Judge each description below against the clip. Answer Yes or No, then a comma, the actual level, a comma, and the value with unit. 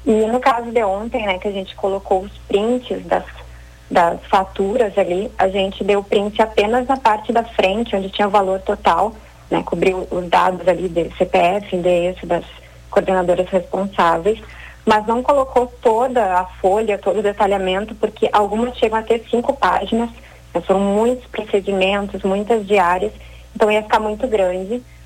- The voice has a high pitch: Yes, high, 200 Hz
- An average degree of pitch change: Yes, average, 3.1 semitones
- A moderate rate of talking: Yes, average, 160 wpm